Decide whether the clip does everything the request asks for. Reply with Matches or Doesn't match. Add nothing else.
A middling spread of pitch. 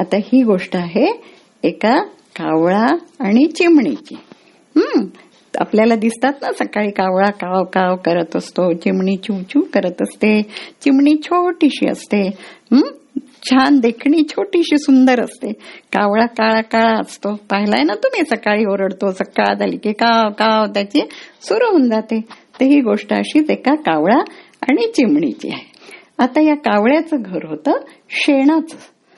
Doesn't match